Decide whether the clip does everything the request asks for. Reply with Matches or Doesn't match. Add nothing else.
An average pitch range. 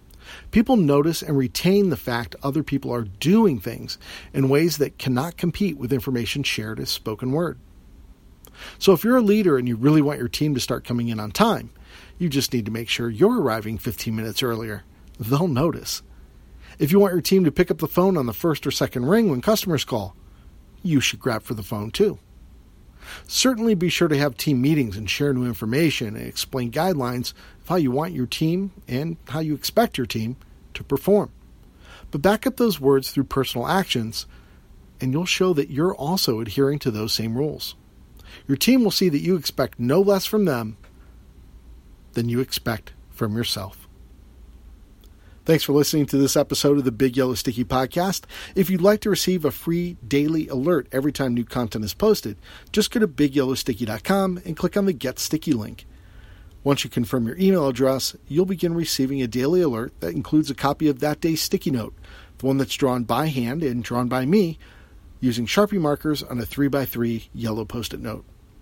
Doesn't match